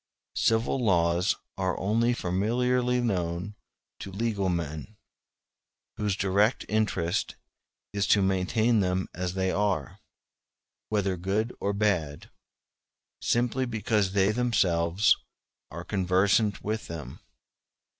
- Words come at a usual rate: No, slow, 105 wpm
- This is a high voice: No, low, 100 Hz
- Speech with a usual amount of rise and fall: Yes, average, 3.1 semitones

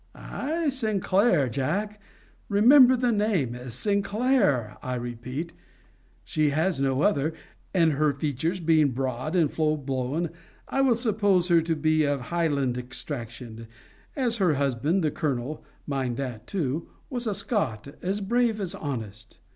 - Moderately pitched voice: Yes, medium, 155 Hz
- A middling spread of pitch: No, wide, 7.3 semitones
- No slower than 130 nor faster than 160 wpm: Yes, average, 140 wpm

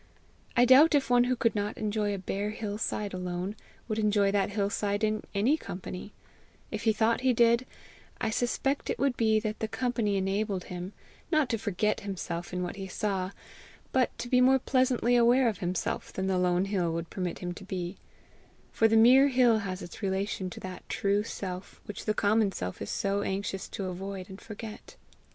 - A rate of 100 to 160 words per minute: No, average, 195 wpm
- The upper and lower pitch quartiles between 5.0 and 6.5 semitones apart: No, average, 3.3 semitones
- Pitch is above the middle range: Yes, high, 205 Hz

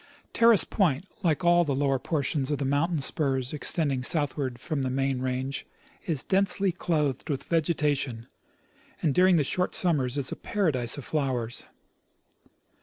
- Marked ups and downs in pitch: No, average, 4.2 semitones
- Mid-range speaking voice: Yes, medium, 145 Hz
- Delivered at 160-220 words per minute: No, average, 150 wpm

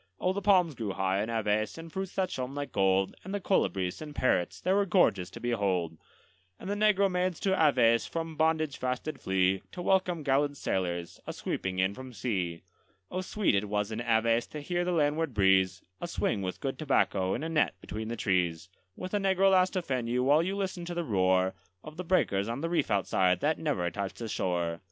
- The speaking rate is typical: No, fast, 215 wpm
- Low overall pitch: Yes, low, 130 Hz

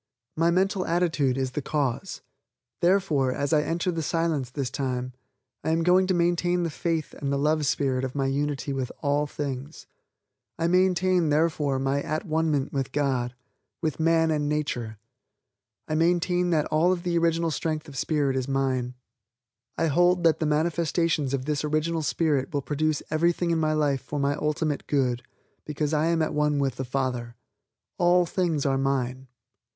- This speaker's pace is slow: No, average, 175 wpm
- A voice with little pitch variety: No, average, 3.4 semitones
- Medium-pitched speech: Yes, medium, 150 Hz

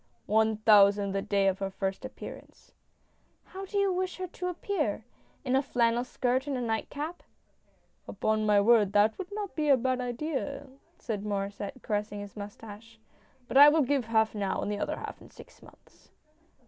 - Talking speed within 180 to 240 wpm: Yes, average, 200 wpm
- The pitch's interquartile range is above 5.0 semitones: Yes, wide, 5.6 semitones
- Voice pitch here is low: No, high, 230 Hz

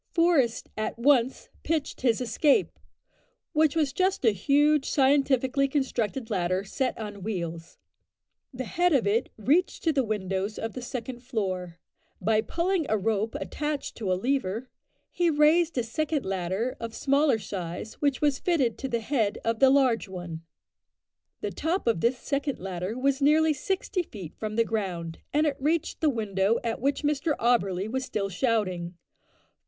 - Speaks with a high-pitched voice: Yes, high, 245 Hz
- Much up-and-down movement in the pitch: Yes, wide, 5.7 semitones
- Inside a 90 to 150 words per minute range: No, average, 160 wpm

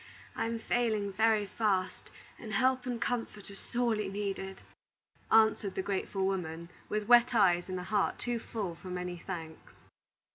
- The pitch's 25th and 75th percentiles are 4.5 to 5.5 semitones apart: No, average, 3.3 semitones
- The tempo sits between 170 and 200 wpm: No, average, 155 wpm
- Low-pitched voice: No, high, 205 Hz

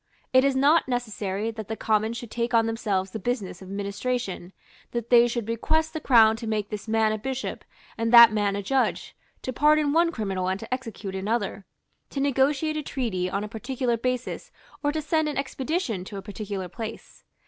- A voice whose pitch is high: Yes, high, 230 Hz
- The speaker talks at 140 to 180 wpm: No, average, 195 wpm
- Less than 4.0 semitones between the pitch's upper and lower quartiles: No, average, 4.3 semitones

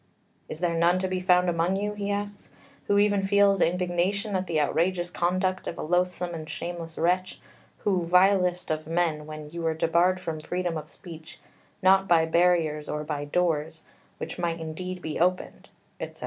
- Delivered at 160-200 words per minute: Yes, average, 175 wpm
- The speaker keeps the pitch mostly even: Yes, narrow, 2.3 semitones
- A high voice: No, medium, 175 Hz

